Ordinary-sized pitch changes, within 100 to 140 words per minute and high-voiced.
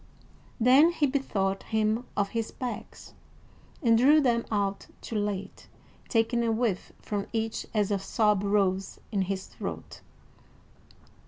Yes: average, 3.1 semitones; slow, 135 wpm; high, 220 Hz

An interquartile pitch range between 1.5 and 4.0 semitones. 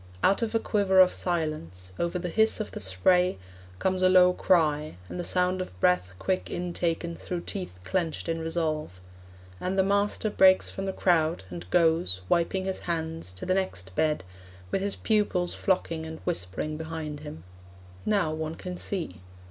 Yes: average, 3.4 semitones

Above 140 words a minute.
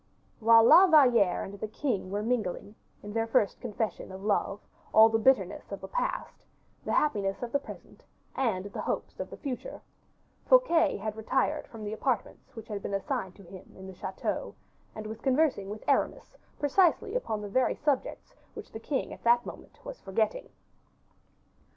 Yes: average, 175 wpm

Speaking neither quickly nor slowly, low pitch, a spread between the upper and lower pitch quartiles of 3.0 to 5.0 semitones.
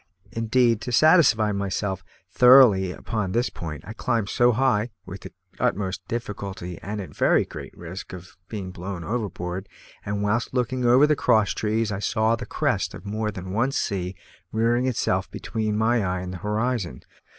Yes: average, 170 wpm; low, 105 Hz; average, 3.8 semitones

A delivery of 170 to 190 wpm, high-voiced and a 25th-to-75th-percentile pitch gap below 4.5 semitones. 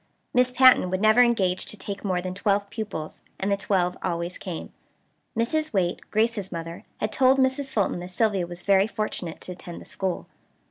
Yes: average, 185 wpm; high, 200 Hz; average, 4.1 semitones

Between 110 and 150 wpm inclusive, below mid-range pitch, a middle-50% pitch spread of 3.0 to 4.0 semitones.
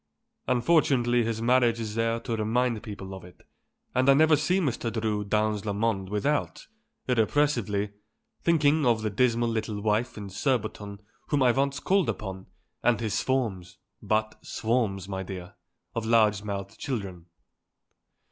Yes: average, 145 wpm; low, 115 Hz; average, 3.6 semitones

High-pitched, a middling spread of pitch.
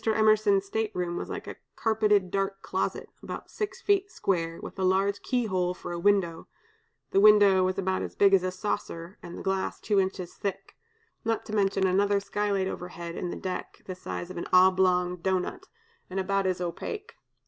No: high, 195 Hz; narrow, 2.1 semitones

